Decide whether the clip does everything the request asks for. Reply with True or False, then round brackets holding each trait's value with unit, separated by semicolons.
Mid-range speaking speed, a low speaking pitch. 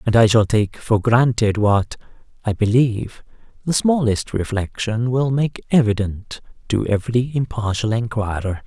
False (130 wpm; 115 Hz)